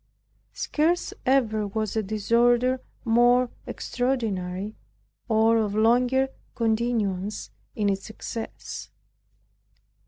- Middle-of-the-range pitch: No, high, 225 Hz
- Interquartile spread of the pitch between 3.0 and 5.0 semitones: No, narrow, 2.6 semitones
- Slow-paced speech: Yes, slow, 85 wpm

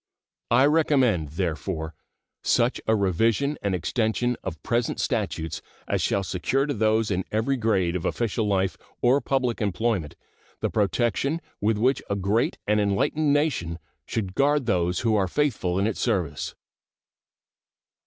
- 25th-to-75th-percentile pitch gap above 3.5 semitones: Yes, average, 4.8 semitones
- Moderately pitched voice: No, low, 110 Hz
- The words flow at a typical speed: Yes, average, 145 wpm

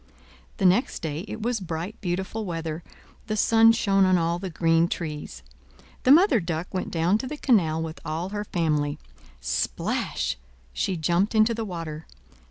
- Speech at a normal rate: Yes, average, 165 wpm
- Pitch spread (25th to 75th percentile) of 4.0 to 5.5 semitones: Yes, average, 4.8 semitones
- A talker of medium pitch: Yes, medium, 180 Hz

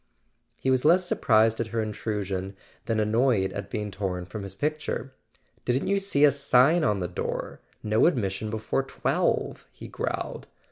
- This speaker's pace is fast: No, average, 170 wpm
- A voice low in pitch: Yes, low, 110 Hz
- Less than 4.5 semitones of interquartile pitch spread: No, average, 5.1 semitones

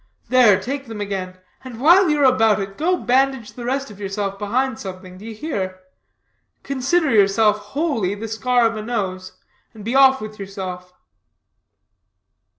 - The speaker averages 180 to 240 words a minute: No, average, 155 wpm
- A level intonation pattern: No, average, 5.0 semitones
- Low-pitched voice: No, high, 220 Hz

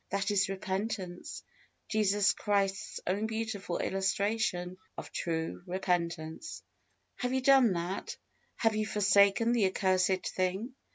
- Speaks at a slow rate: Yes, slow, 115 wpm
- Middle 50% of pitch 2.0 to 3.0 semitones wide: Yes, average, 2.7 semitones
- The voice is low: No, high, 195 Hz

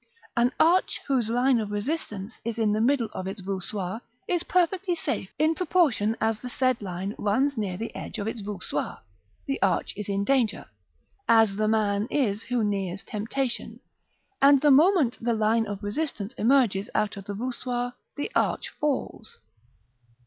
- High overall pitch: Yes, high, 225 Hz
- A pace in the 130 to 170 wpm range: Yes, average, 165 wpm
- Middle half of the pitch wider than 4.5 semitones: Yes, average, 4.9 semitones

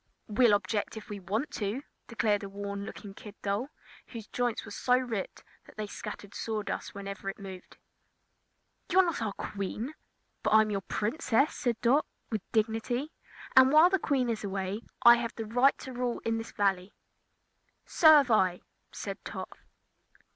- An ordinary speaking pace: Yes, average, 165 wpm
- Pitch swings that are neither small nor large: Yes, average, 3.6 semitones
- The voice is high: Yes, high, 220 Hz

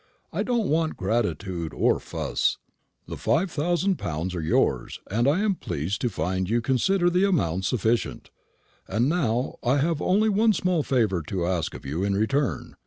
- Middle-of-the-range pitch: No, low, 120 Hz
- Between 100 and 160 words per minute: No, average, 175 wpm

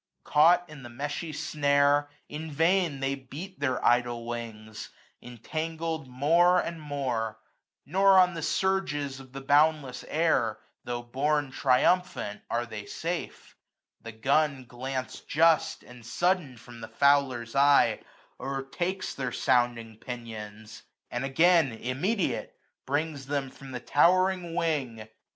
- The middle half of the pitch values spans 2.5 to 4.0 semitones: No, average, 4.8 semitones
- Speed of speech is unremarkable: No, slow, 130 wpm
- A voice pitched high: No, medium, 140 Hz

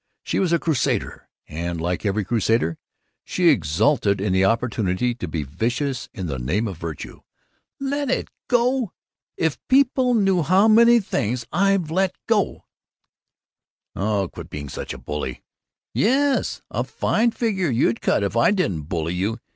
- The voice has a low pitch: Yes, low, 120 Hz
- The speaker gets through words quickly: No, average, 155 wpm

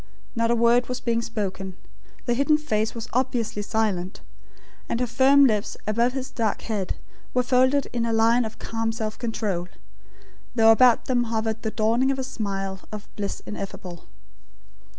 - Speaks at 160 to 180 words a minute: Yes, average, 165 wpm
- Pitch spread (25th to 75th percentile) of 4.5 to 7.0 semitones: No, narrow, 2.6 semitones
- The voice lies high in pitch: Yes, high, 230 Hz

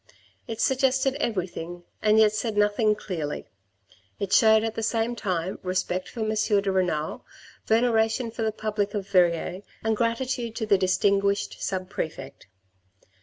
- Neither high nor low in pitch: No, high, 210 Hz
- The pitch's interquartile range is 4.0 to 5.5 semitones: No, average, 3.2 semitones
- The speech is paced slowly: No, average, 145 wpm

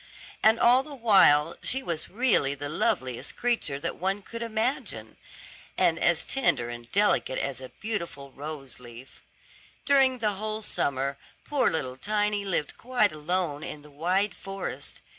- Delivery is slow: No, average, 150 wpm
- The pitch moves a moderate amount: No, wide, 7.6 semitones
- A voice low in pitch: No, medium, 185 Hz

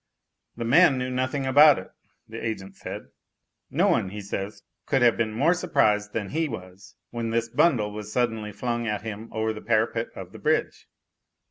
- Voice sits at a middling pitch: No, low, 115 Hz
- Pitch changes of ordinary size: Yes, average, 3.4 semitones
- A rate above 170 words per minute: Yes, average, 185 wpm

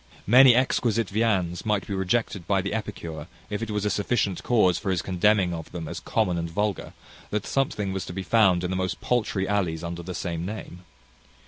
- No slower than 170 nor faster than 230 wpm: Yes, fast, 205 wpm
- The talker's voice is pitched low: Yes, very low, 95 Hz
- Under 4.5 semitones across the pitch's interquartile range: Yes, average, 3.2 semitones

